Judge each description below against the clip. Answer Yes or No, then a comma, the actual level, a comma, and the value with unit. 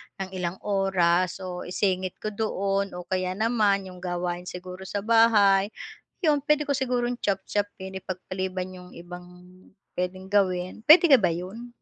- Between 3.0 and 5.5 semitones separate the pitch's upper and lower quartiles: No, narrow, 2.4 semitones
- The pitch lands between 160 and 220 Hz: Yes, high, 190 Hz